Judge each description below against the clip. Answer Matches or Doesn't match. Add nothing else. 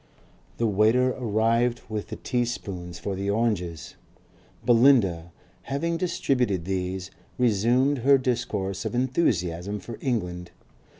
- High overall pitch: Doesn't match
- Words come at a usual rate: Doesn't match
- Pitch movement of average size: Matches